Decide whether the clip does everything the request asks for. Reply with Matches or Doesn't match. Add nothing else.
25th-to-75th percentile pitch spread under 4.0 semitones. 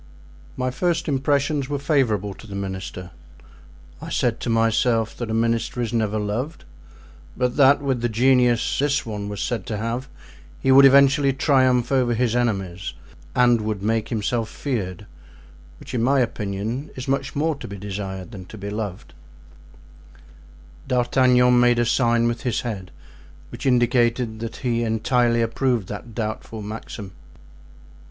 Matches